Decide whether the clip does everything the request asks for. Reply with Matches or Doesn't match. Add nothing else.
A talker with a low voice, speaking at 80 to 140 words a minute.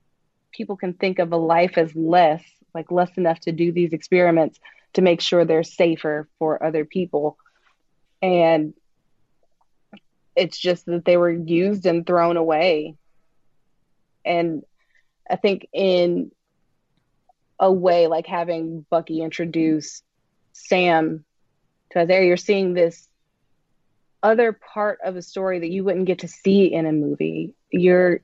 Doesn't match